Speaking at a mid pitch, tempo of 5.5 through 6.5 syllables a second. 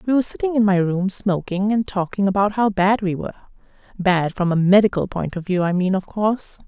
No: high, 195 Hz; 5.8 syllables/s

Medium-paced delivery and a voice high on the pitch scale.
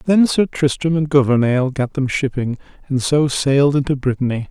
No: average, 175 wpm; medium, 140 Hz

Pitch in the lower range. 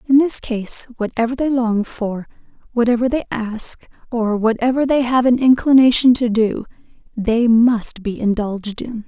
No: high, 235 Hz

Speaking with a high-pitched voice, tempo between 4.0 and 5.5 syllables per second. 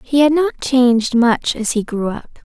Yes: very high, 250 Hz; 4.7 syllables/s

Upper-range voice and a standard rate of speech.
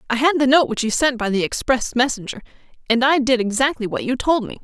No: very high, 250 Hz; fast, 245 wpm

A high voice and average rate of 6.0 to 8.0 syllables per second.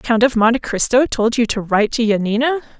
Yes: high, 235 Hz; 6.2 syllables/s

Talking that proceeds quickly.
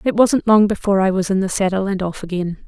Yes: fast, 270 wpm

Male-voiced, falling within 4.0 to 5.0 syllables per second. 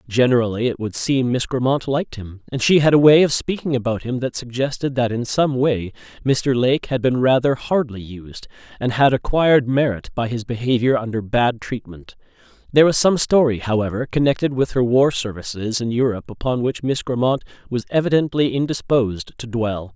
No: male; 5.4 syllables/s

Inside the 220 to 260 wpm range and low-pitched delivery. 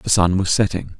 Yes: fast, 240 wpm; very low, 95 Hz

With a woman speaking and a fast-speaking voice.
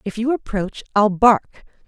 No: female; average, 160 wpm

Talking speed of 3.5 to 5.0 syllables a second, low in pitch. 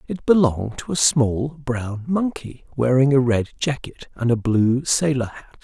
Yes: 4.3 syllables/s; low, 130 Hz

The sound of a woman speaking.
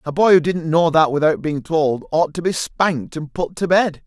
No: male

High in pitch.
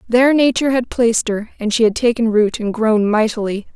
Yes: high, 225 Hz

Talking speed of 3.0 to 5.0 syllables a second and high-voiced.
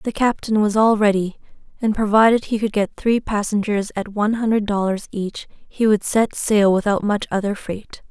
Yes: 4.9 syllables/s; high, 210 Hz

